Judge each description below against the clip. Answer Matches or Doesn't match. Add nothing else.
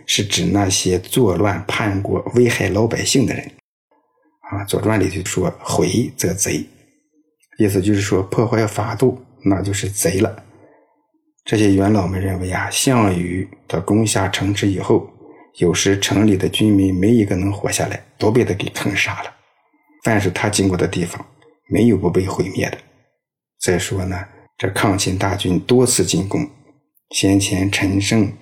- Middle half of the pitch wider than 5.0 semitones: Doesn't match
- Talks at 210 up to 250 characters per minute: Matches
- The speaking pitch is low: Matches